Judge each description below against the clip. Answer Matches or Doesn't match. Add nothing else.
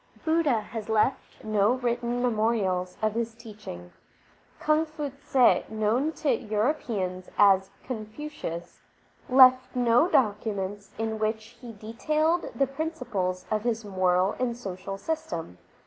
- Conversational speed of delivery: Doesn't match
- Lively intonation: Doesn't match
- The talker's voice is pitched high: Matches